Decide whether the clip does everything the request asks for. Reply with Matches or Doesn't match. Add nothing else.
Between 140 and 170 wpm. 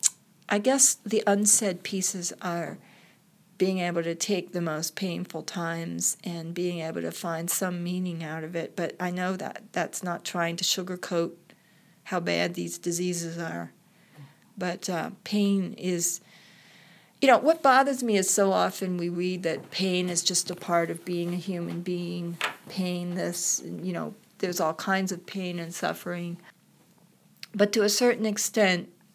Matches